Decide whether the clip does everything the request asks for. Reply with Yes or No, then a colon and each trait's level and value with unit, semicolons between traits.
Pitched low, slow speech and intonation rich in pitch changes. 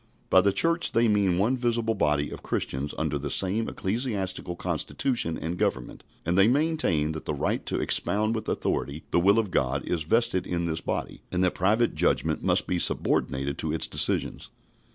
No: very low, 95 Hz; average, 185 wpm; wide, 6.1 semitones